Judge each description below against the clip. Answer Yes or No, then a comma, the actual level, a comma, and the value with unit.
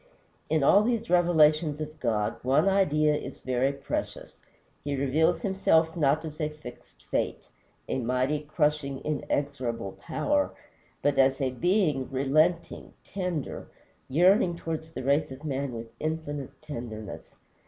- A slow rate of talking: Yes, slow, 130 wpm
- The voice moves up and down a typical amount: Yes, average, 3.3 semitones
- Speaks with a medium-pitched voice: Yes, medium, 150 Hz